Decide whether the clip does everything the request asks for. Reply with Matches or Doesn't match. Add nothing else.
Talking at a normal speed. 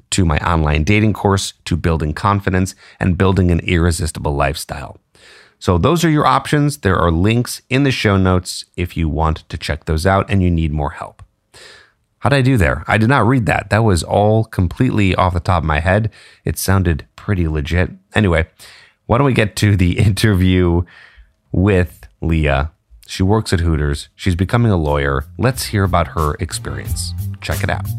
Matches